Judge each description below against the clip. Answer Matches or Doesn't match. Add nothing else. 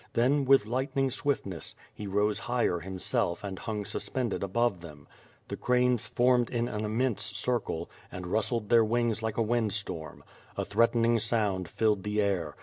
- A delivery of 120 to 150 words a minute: Doesn't match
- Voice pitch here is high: Doesn't match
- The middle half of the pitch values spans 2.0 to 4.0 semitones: Matches